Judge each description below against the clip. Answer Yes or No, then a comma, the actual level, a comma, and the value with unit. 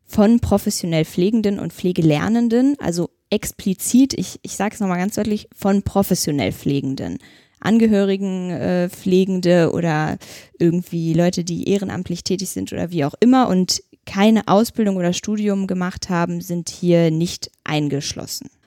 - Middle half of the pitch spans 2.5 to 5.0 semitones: Yes, average, 3.3 semitones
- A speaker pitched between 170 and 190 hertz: Yes, medium, 185 Hz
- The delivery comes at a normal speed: Yes, average, 135 wpm